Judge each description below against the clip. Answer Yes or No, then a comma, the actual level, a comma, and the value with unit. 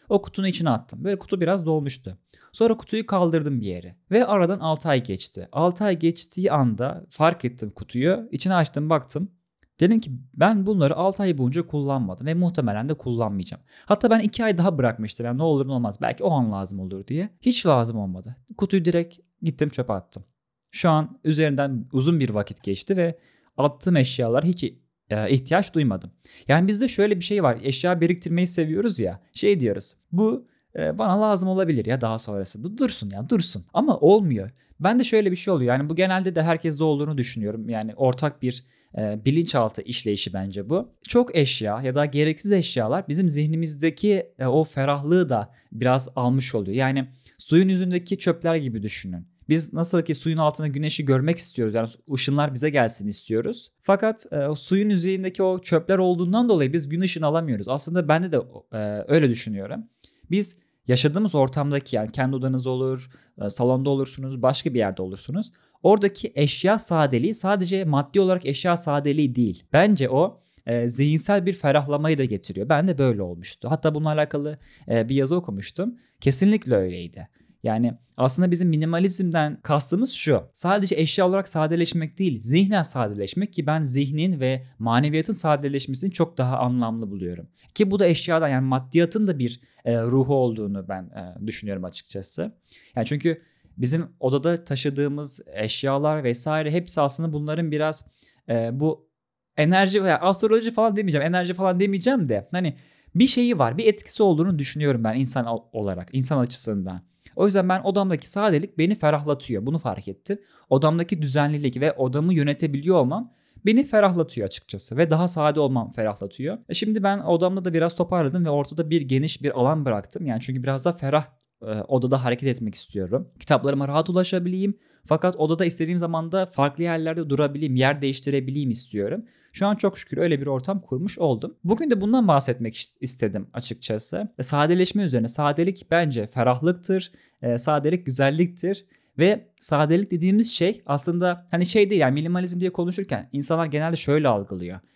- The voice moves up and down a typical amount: No, wide, 6.1 semitones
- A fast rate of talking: Yes, fast, 160 wpm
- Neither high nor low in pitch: Yes, medium, 150 Hz